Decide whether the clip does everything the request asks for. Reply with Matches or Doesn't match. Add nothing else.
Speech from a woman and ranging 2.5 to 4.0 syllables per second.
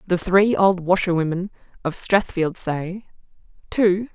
Matches